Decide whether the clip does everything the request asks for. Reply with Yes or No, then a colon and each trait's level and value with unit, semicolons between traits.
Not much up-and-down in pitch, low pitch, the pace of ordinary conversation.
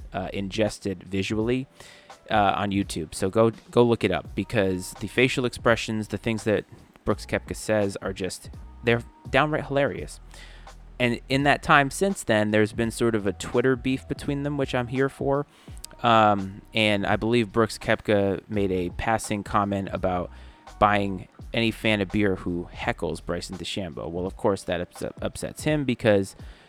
No: average, 3.7 semitones; low, 105 Hz; average, 165 wpm